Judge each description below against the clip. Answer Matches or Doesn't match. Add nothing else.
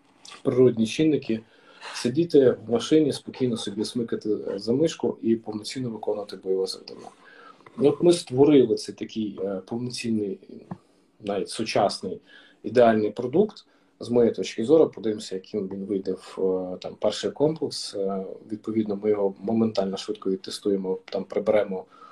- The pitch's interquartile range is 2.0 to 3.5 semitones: Doesn't match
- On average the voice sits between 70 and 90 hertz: Doesn't match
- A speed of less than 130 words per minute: Matches